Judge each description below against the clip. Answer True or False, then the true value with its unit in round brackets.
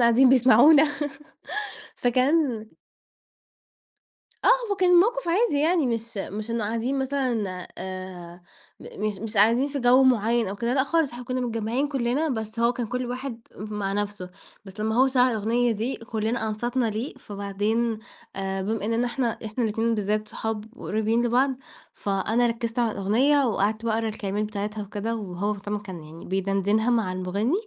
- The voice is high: True (225 Hz)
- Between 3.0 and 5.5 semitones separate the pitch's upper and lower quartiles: True (3.3 semitones)